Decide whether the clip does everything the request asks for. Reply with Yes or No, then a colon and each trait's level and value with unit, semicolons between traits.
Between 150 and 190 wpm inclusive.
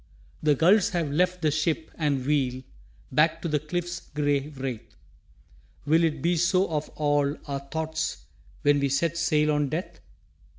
Yes: average, 160 wpm